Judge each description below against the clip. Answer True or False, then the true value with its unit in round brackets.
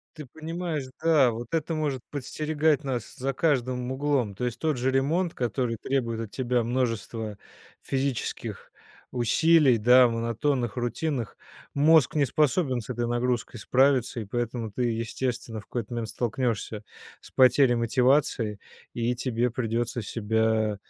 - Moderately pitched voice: False (125 Hz)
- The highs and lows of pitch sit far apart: False (3.3 semitones)